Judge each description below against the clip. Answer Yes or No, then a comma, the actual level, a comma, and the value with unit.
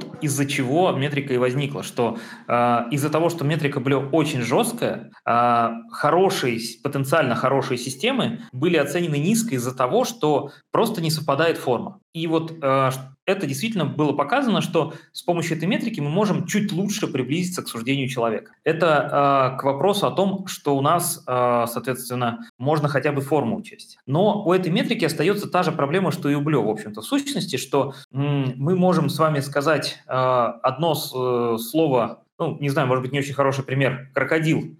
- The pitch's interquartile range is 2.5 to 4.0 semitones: No, average, 4.6 semitones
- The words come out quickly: Yes, fast, 165 wpm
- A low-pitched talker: No, medium, 145 Hz